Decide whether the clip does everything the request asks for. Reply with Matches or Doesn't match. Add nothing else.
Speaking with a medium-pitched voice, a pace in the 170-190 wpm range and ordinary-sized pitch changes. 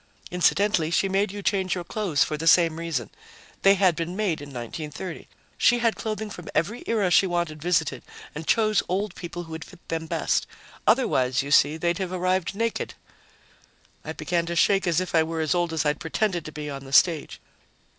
Doesn't match